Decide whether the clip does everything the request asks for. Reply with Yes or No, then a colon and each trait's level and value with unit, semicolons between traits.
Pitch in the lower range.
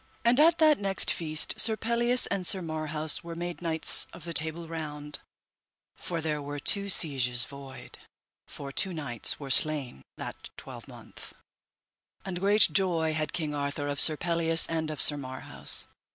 No: medium, 160 Hz